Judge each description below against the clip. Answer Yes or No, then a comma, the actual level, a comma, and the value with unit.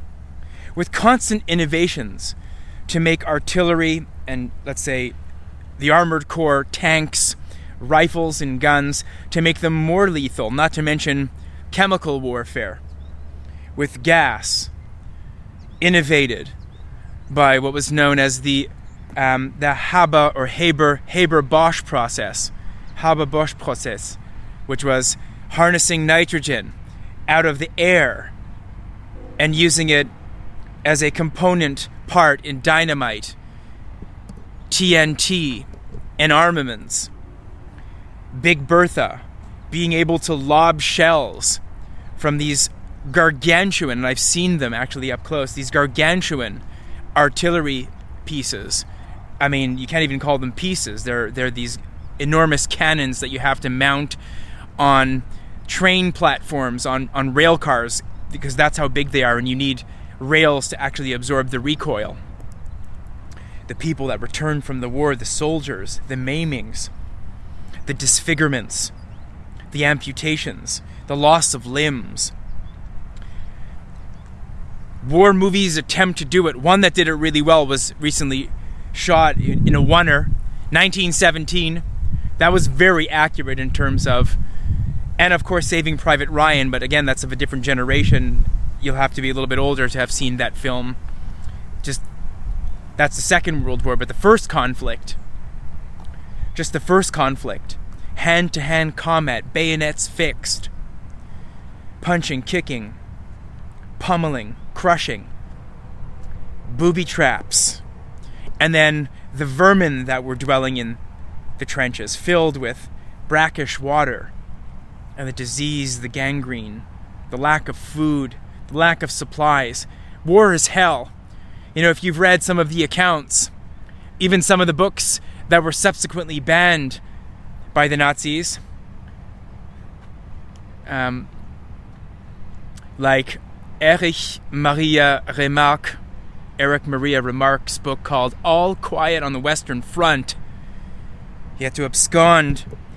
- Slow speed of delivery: Yes, slow, 125 wpm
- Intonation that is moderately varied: No, wide, 7.6 semitones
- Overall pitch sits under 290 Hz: Yes, low, 135 Hz